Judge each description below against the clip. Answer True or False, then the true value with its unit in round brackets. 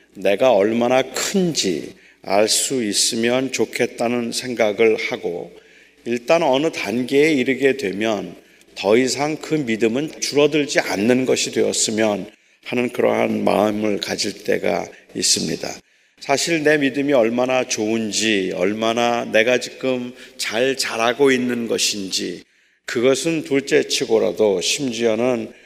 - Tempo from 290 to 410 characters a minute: False (255 characters per minute)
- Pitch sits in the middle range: False (125 Hz)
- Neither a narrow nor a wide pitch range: True (4.3 semitones)